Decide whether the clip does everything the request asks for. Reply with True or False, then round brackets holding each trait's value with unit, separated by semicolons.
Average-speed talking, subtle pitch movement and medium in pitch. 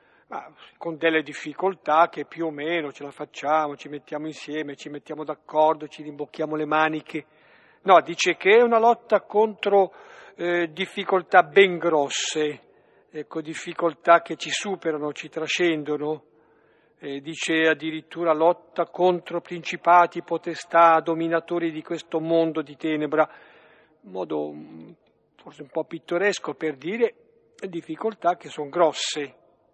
True (130 wpm; 2.3 semitones; 160 Hz)